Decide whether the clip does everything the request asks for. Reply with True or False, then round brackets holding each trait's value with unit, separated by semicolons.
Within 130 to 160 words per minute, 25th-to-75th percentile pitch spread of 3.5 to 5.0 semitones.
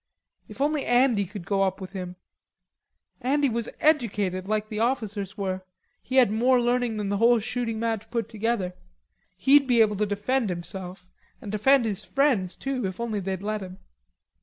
False (175 wpm; 4.0 semitones)